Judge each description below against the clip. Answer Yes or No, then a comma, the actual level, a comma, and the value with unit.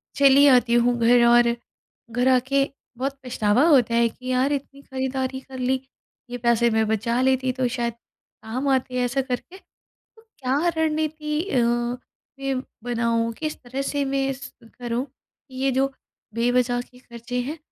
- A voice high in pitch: Yes, very high, 255 Hz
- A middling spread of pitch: No, narrow, 2.2 semitones